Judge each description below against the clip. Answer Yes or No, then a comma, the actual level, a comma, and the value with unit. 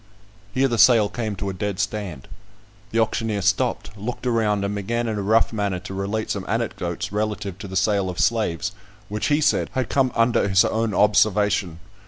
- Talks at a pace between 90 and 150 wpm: No, average, 190 wpm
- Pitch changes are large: No, narrow, 2.4 semitones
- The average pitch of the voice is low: Yes, low, 105 Hz